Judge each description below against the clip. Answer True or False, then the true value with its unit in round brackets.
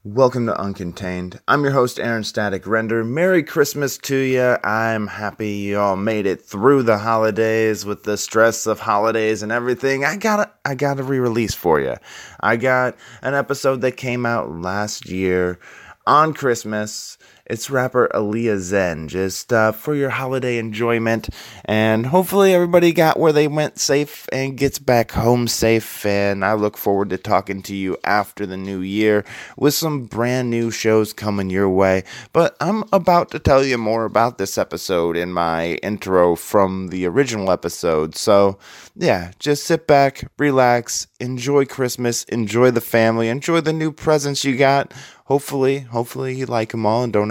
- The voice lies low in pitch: True (115 Hz)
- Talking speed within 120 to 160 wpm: False (170 wpm)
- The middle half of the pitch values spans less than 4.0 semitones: False (4.7 semitones)